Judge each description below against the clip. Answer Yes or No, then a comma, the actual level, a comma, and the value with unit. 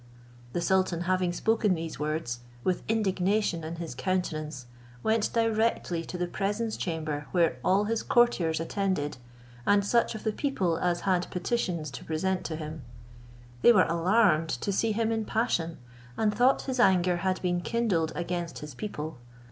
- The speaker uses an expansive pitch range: No, average, 4.5 semitones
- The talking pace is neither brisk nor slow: Yes, average, 160 wpm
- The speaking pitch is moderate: Yes, medium, 180 Hz